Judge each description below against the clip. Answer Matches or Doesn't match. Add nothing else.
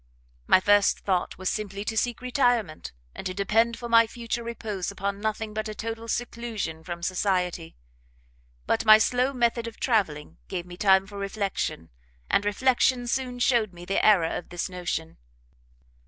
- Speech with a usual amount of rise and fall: Matches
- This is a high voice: Matches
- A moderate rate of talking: Matches